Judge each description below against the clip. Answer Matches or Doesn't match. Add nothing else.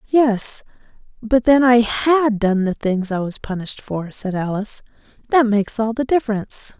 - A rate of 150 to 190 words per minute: Matches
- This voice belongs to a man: Doesn't match